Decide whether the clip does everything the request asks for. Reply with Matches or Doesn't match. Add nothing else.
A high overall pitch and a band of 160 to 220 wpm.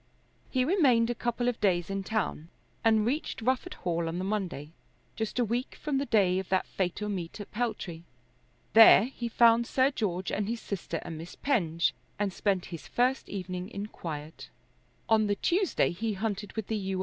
Matches